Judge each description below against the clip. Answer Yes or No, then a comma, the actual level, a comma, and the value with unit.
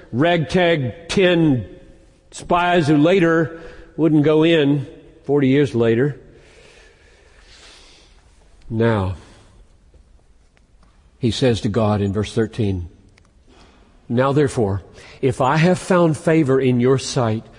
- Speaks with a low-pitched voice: Yes, low, 125 Hz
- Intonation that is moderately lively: No, wide, 7.6 semitones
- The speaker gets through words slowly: Yes, slow, 100 wpm